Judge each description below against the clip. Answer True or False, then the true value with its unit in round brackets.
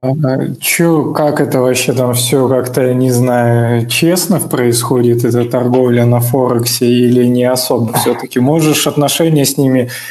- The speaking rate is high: False (140 wpm)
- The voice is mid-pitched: False (125 Hz)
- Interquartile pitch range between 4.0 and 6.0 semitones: False (2.7 semitones)